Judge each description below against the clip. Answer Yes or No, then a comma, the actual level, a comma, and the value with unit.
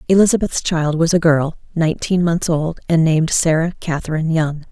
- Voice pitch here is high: No, medium, 165 Hz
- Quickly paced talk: No, average, 165 wpm